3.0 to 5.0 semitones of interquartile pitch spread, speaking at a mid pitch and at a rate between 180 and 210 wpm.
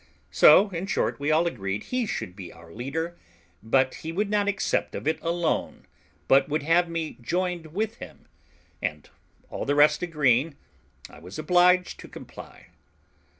No: average, 4.6 semitones; medium, 160 Hz; average, 160 wpm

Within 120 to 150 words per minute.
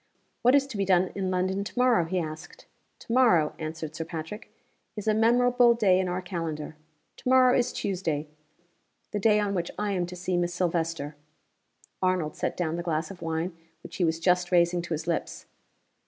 No: average, 195 wpm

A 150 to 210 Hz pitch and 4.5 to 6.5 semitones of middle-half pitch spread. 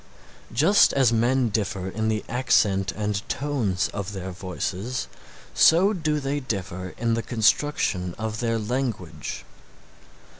No: low, 110 Hz; average, 5.1 semitones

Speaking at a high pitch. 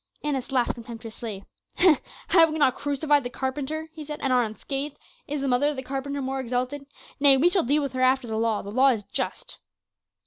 Yes: very high, 270 Hz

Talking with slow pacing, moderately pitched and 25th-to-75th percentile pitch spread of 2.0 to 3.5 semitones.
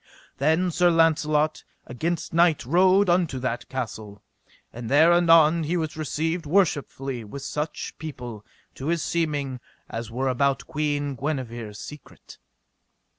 No: slow, 125 wpm; medium, 150 Hz; average, 4.2 semitones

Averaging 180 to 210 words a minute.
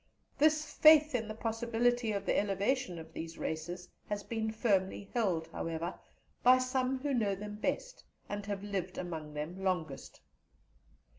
No: average, 155 wpm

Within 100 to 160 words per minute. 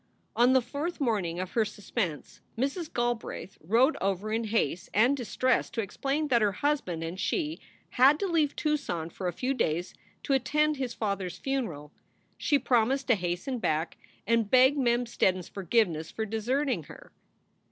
No: average, 170 wpm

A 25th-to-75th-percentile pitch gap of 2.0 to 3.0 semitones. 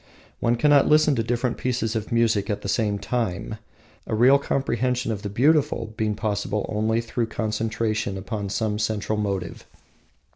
Yes: narrow, 2.4 semitones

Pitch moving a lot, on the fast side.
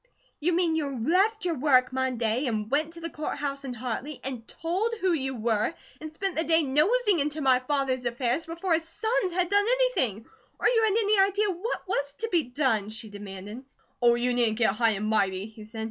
Yes: wide, 6.7 semitones; fast, 215 wpm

